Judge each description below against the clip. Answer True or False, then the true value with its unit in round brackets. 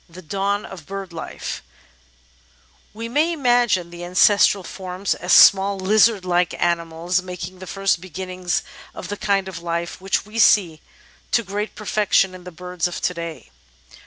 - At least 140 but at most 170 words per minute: True (160 wpm)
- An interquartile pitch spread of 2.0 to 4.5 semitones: True (2.4 semitones)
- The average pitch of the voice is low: False (185 Hz)